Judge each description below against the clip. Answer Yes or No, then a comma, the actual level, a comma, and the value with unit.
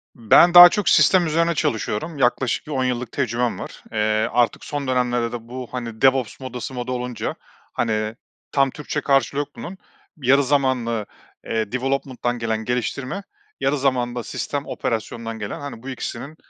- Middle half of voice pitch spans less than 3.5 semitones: Yes, average, 3.0 semitones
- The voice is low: Yes, low, 125 Hz